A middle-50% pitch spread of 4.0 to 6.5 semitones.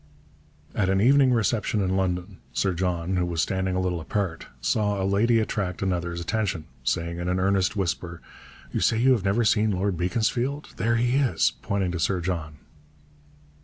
No: average, 3.5 semitones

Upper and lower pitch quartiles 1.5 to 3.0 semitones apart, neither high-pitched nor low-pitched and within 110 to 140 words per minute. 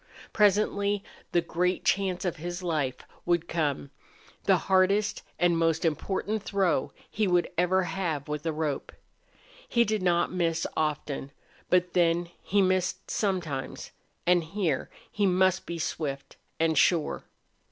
Yes: average, 2.7 semitones; medium, 175 Hz; slow, 135 wpm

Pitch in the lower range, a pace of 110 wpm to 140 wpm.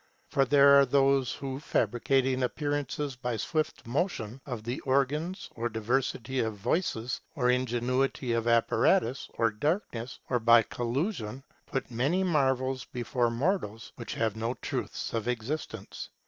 Yes: low, 125 Hz; slow, 135 wpm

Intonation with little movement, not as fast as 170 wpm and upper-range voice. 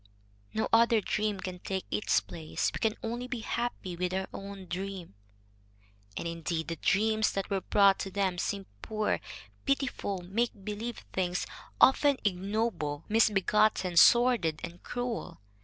No: average, 3.7 semitones; average, 140 wpm; high, 195 Hz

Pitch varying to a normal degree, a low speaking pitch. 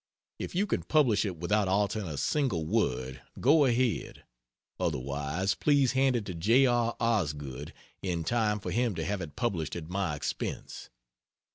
No: wide, 6.6 semitones; low, 100 Hz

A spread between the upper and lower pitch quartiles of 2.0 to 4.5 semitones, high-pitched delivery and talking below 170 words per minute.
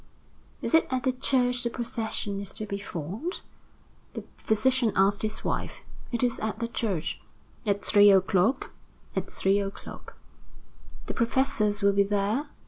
Yes: average, 3.7 semitones; high, 215 Hz; average, 150 wpm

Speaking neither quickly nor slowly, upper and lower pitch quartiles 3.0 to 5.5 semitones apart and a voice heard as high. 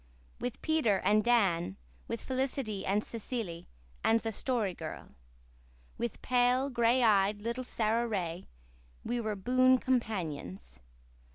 No: slow, 120 wpm; average, 4.0 semitones; high, 225 Hz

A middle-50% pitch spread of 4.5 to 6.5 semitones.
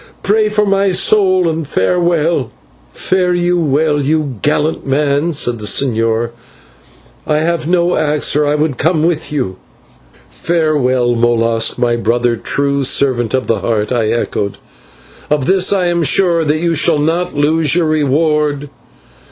Yes: average, 5.1 semitones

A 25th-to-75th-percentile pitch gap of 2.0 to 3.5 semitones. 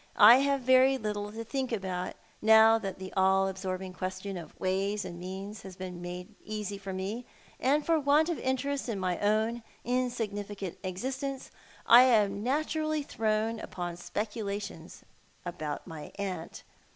No: average, 4.9 semitones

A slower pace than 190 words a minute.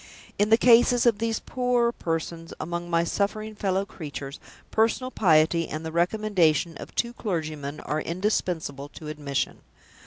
Yes: average, 145 wpm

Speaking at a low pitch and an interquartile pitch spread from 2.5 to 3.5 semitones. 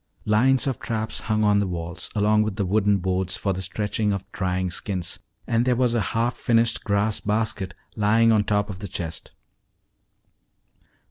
Yes: low, 105 Hz; average, 2.9 semitones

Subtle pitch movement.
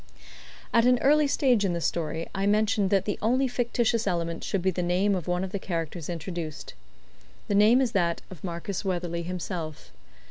No: average, 4.1 semitones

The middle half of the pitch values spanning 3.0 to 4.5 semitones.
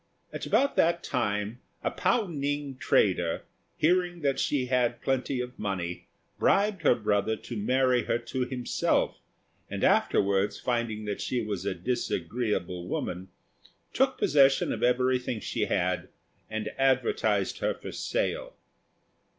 No: average, 5.2 semitones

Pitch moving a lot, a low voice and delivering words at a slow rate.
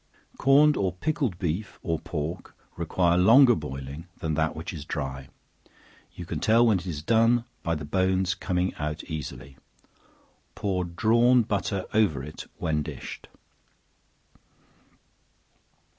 Yes: wide, 5.9 semitones; very low, 90 Hz; slow, 130 wpm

